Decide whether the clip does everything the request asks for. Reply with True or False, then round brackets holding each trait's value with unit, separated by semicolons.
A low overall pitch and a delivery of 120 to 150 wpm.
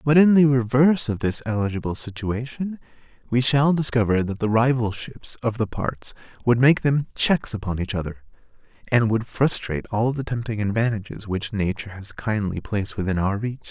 False (115 Hz; 170 wpm)